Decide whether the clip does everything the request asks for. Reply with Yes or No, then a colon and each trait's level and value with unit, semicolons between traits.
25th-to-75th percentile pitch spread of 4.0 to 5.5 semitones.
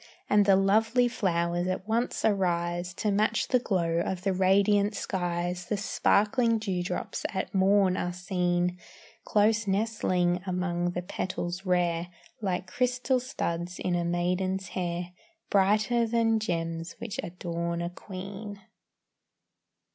No: average, 2.9 semitones